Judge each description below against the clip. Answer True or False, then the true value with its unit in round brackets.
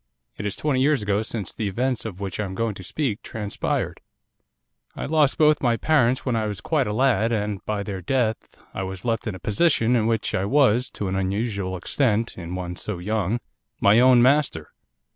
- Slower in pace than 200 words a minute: False (205 wpm)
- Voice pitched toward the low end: True (110 Hz)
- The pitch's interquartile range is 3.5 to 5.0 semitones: True (4.2 semitones)